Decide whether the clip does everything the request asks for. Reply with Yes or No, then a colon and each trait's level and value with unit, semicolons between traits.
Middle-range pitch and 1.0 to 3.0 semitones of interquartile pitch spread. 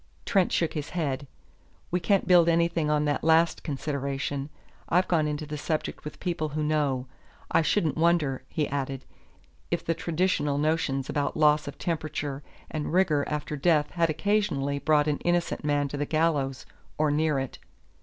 Yes: medium, 150 Hz; narrow, 2.6 semitones